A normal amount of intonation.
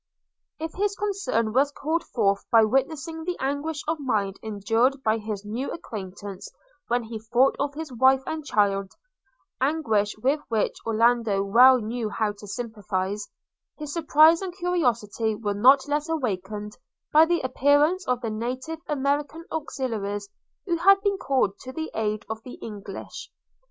No: wide, 6.0 semitones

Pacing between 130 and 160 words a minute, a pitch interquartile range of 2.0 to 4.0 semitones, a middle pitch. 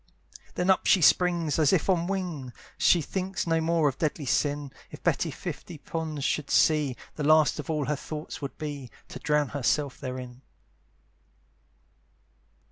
Yes: average, 155 wpm; average, 2.7 semitones; medium, 150 Hz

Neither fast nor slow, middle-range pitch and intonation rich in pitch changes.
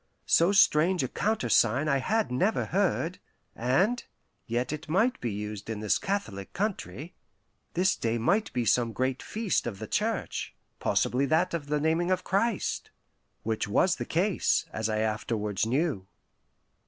Yes: average, 155 wpm; medium, 150 Hz; wide, 8.5 semitones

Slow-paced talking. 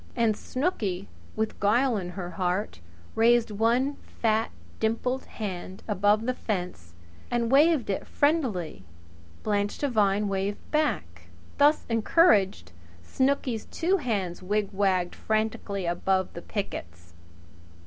Yes: slow, 110 wpm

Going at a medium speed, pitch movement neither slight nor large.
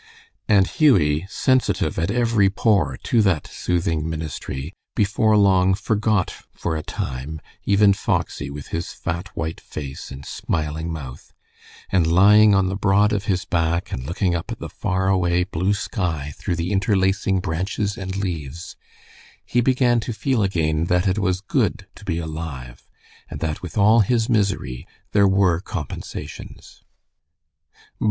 Yes: average, 150 wpm; average, 4.1 semitones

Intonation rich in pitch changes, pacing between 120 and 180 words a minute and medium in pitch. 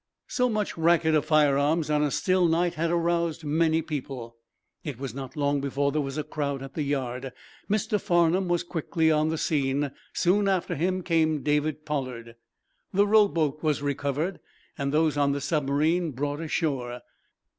No: average, 3.0 semitones; average, 165 wpm; medium, 155 Hz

